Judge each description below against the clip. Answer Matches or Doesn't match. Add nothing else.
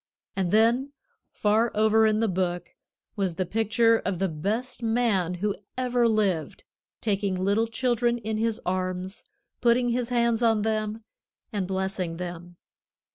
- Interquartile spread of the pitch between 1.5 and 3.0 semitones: Doesn't match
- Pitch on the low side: Doesn't match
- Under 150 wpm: Matches